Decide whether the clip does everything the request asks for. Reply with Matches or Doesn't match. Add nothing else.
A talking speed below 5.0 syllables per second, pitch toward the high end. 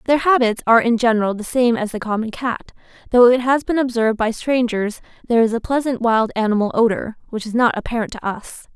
Doesn't match